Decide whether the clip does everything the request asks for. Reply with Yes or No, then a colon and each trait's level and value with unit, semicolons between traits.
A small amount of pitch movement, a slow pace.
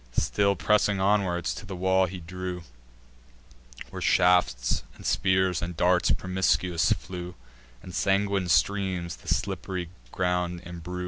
Yes: narrow, 1.5 semitones; slow, 125 wpm